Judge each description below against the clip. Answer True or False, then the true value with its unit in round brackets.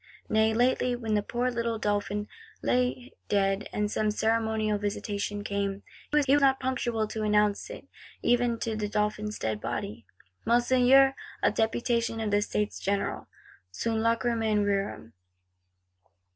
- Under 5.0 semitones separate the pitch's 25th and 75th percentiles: True (2.5 semitones)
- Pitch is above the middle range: True (220 Hz)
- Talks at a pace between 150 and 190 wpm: False (135 wpm)